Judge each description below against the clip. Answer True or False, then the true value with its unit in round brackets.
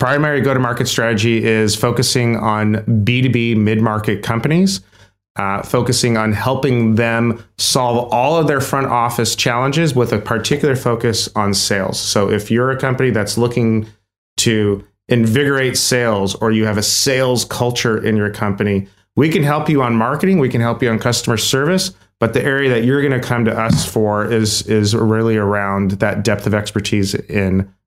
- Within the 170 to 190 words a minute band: True (175 wpm)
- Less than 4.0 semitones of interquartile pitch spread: True (3.1 semitones)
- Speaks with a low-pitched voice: True (115 Hz)